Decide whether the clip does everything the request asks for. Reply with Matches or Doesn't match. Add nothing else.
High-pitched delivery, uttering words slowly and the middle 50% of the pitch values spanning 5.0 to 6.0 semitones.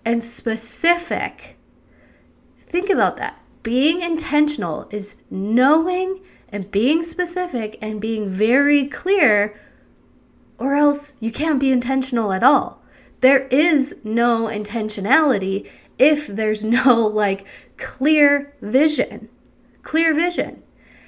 Matches